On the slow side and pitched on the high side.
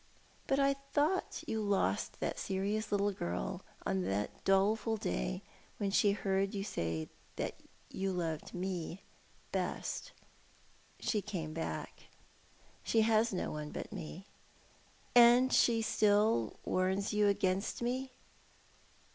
Yes: slow, 120 wpm; high, 200 Hz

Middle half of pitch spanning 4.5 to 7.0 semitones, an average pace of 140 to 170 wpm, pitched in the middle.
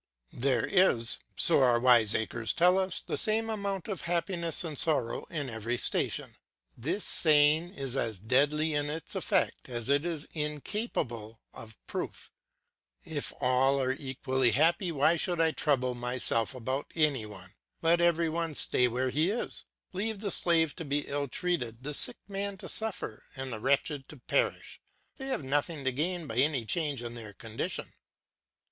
Yes: wide, 5.4 semitones; average, 165 wpm; medium, 145 Hz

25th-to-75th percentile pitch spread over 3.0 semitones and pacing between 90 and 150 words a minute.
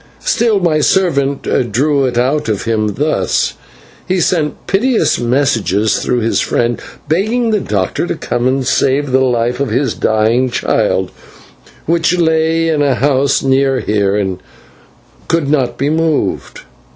Yes: average, 5.1 semitones; average, 145 wpm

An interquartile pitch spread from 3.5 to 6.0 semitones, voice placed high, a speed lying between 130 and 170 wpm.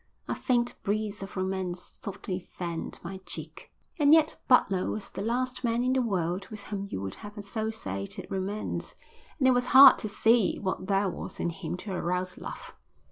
No: average, 4.0 semitones; high, 200 Hz; average, 185 wpm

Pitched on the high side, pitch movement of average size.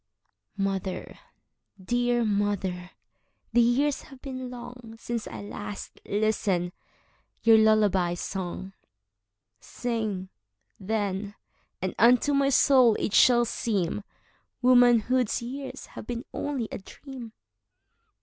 Yes: high, 220 Hz; average, 4.0 semitones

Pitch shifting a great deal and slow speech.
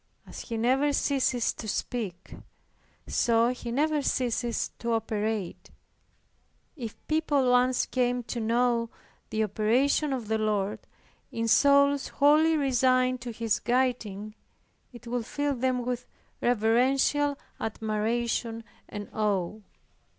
No: average, 2.9 semitones; slow, 115 wpm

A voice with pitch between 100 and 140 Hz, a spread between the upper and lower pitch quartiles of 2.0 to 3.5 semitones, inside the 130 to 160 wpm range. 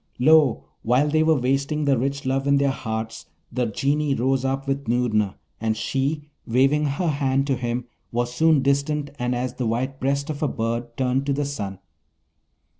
No: low, 135 Hz; narrow, 2.6 semitones; average, 185 wpm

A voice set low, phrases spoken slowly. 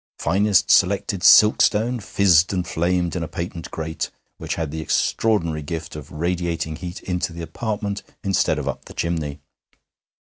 No: very low, 85 Hz; average, 150 wpm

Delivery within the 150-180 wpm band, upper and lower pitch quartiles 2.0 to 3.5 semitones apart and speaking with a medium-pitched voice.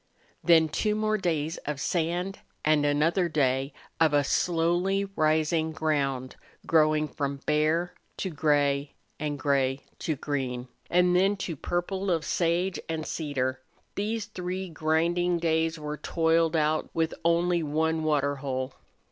No: average, 140 wpm; average, 3.1 semitones; medium, 160 Hz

